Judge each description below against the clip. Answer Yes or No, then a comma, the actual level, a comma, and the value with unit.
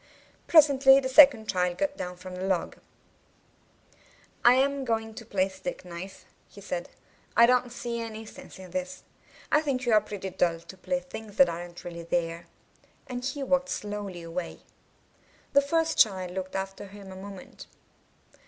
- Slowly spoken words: No, average, 165 wpm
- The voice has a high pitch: Yes, high, 210 Hz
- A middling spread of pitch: No, wide, 6.2 semitones